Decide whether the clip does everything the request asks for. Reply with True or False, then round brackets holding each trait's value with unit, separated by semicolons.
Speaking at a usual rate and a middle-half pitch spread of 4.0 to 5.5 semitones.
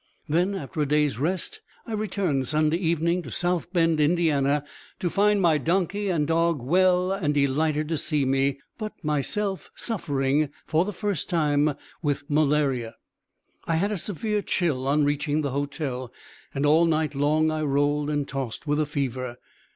False (160 wpm; 3.6 semitones)